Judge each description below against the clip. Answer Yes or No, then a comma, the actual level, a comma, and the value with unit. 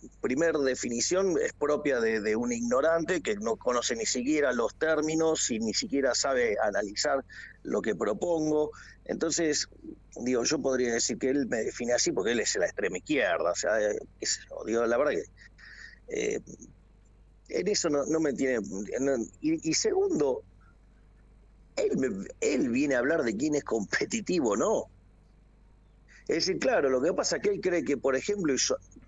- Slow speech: No, average, 170 wpm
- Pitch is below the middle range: No, medium, 175 Hz